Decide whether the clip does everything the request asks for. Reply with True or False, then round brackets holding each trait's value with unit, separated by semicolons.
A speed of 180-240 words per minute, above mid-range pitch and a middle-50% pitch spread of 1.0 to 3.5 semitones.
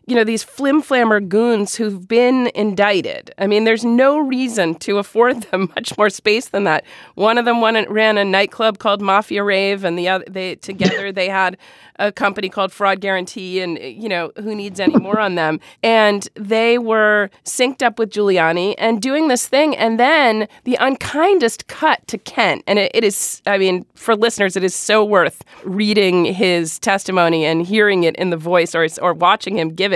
True (195 wpm; 205 Hz; 3.2 semitones)